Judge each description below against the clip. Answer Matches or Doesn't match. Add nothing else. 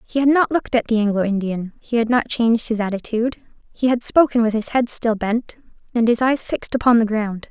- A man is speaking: Doesn't match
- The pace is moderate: Doesn't match